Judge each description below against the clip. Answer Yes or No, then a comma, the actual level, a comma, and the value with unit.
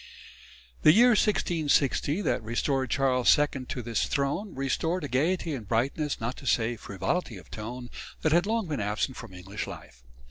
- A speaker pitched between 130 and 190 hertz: Yes, low, 135 Hz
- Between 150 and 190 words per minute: Yes, average, 170 wpm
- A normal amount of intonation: No, wide, 5.8 semitones